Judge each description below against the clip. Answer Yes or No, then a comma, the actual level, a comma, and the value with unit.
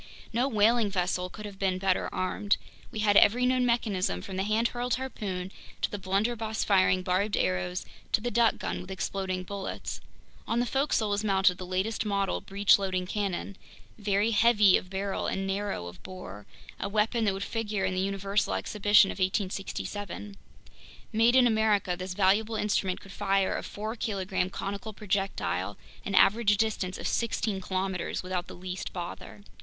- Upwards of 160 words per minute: Yes, average, 170 wpm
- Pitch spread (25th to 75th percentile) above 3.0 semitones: No, narrow, 2.5 semitones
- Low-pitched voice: No, high, 200 Hz